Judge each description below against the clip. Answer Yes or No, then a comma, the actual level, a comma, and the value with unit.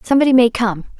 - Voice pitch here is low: No, high, 235 Hz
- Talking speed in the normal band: Yes, average, 180 wpm